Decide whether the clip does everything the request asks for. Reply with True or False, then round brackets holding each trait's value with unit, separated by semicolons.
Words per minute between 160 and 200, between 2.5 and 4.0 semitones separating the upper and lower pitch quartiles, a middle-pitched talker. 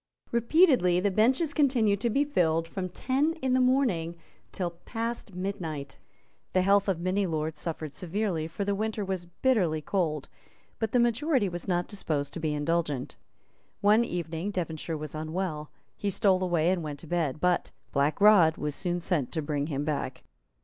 False (170 wpm; 5.0 semitones; 180 Hz)